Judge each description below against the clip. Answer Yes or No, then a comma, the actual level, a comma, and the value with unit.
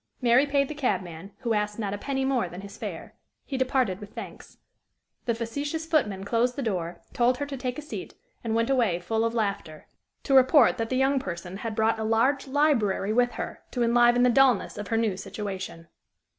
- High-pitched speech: Yes, high, 230 Hz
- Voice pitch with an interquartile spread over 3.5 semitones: Yes, average, 4.6 semitones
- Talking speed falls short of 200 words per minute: No, fast, 205 wpm